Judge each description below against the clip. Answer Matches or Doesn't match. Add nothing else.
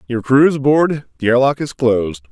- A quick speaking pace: Matches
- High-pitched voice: Doesn't match